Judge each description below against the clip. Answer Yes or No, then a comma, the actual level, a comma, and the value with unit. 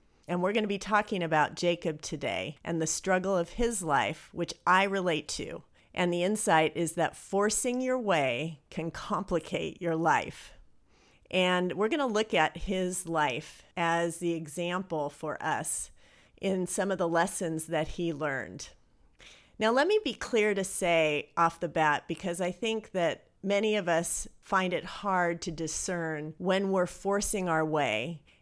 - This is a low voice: No, medium, 175 Hz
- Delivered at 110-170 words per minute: Yes, average, 165 wpm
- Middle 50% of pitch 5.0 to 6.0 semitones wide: No, average, 3.1 semitones